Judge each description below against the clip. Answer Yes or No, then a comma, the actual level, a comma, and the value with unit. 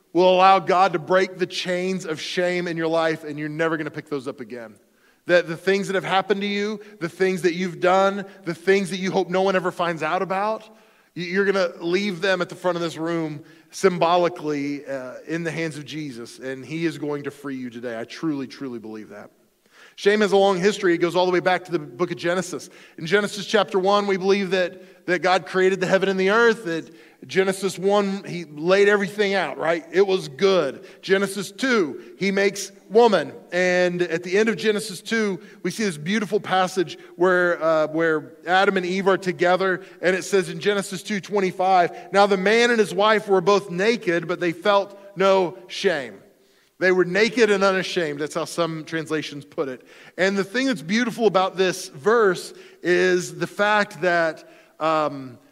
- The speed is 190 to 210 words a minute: Yes, fast, 205 wpm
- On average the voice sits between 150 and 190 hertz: Yes, medium, 185 Hz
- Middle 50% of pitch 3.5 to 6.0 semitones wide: No, average, 3.0 semitones